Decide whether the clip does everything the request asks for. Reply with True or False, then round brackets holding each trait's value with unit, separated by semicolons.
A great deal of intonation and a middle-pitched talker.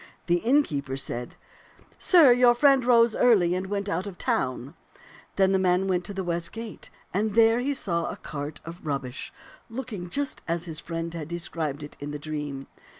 True (6.5 semitones; 180 Hz)